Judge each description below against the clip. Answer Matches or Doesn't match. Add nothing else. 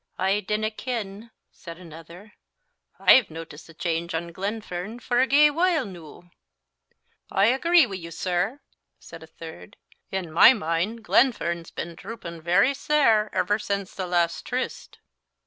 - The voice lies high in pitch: Matches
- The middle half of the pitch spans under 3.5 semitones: Doesn't match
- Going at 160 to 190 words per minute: Doesn't match